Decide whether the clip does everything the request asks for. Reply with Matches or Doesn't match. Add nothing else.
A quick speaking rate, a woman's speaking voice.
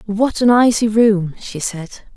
Doesn't match